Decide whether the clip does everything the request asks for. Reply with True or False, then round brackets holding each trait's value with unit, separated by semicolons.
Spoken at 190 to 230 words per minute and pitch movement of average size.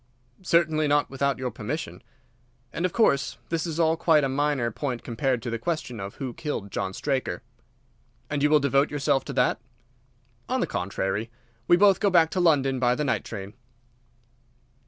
False (175 wpm; 4.5 semitones)